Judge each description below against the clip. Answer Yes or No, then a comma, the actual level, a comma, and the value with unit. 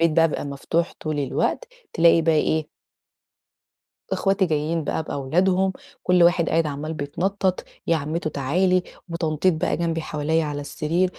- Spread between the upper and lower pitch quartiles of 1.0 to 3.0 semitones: Yes, narrow, 2.5 semitones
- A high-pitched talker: No, medium, 165 Hz